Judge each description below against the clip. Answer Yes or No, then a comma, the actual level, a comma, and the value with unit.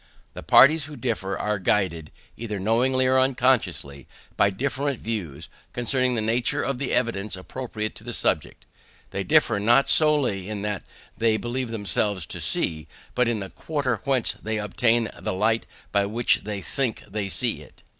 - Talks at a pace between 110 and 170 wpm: Yes, average, 165 wpm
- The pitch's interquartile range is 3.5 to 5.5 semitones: Yes, average, 4.2 semitones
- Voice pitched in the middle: No, low, 115 Hz